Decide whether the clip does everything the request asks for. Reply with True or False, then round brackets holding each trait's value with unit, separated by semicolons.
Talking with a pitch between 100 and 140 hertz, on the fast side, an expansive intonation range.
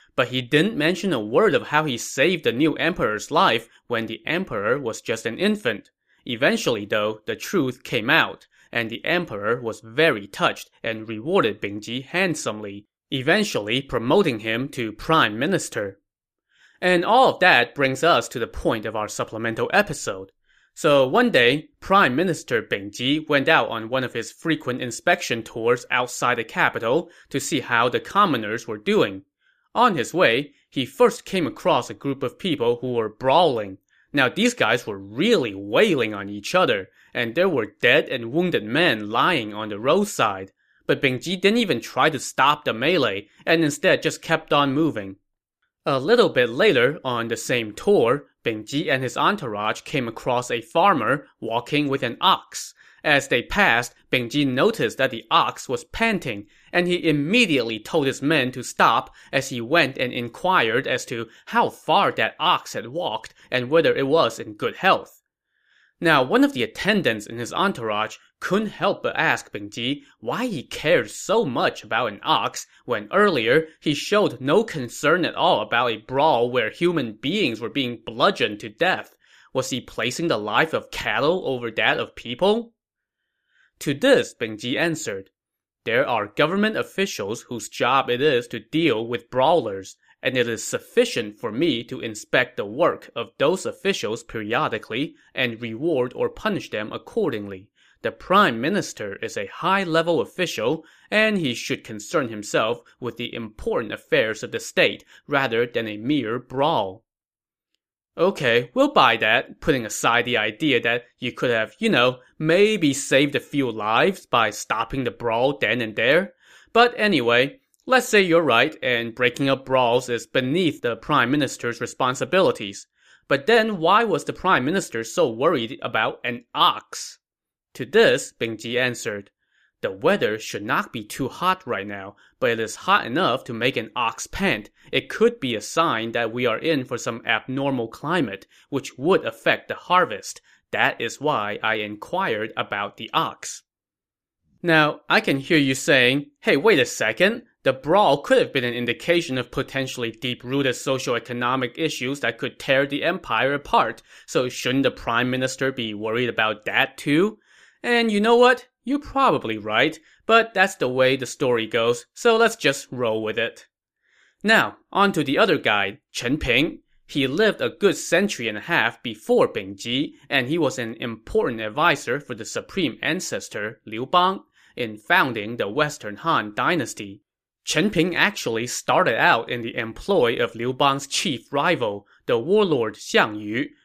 False (135 Hz; 170 wpm; 6.7 semitones)